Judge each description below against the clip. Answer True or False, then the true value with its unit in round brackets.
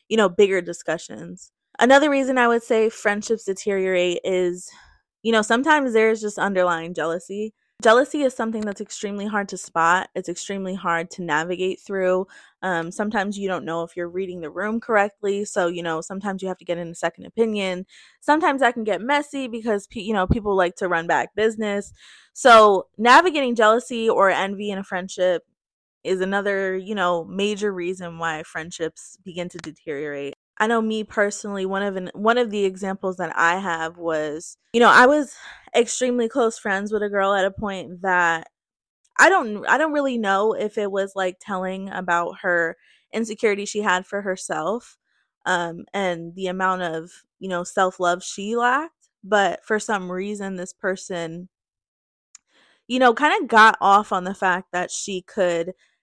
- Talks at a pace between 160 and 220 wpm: True (175 wpm)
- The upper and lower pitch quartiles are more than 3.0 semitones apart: True (3.4 semitones)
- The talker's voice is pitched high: True (195 Hz)